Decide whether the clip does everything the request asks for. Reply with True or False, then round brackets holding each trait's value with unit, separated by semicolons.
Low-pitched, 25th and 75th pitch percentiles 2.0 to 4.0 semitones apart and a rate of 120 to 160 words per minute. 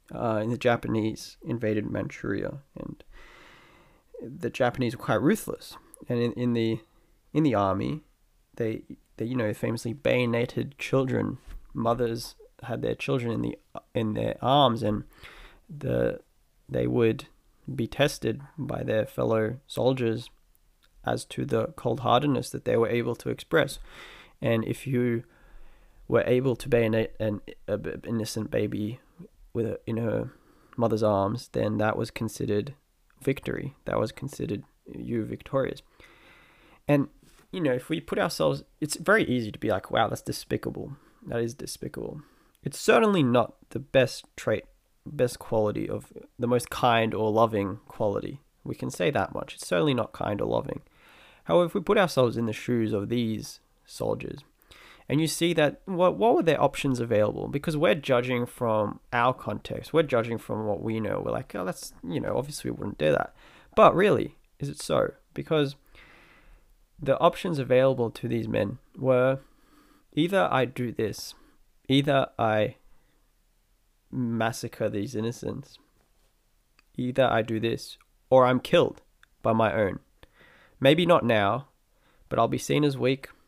True (120 Hz; 3.4 semitones; 150 wpm)